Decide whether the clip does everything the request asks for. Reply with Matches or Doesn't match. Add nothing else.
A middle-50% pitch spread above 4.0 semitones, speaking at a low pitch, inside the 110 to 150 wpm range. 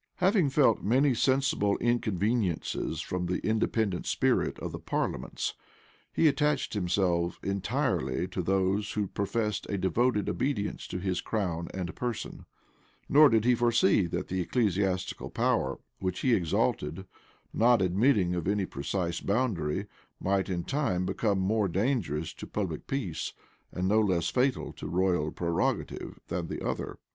Matches